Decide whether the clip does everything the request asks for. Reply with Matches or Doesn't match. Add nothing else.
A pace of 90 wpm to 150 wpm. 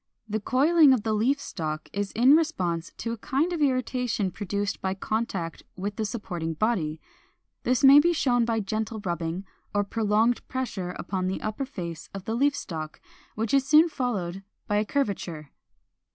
Doesn't match